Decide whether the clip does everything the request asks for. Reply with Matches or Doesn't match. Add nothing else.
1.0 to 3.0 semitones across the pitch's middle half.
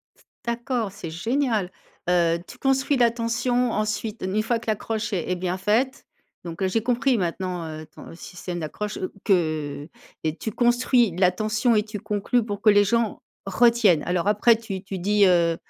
Doesn't match